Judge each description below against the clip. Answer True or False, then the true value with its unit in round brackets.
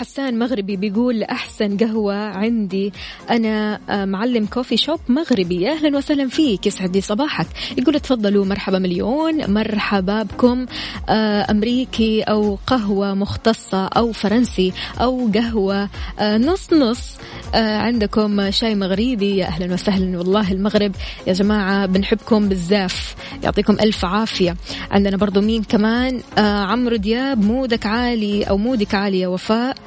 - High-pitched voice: True (210 Hz)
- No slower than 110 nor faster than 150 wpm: True (120 wpm)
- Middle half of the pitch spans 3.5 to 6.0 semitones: False (2.9 semitones)